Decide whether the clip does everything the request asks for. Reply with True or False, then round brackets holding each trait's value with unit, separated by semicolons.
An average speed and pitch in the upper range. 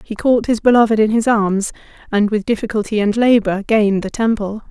True (190 wpm; 215 Hz)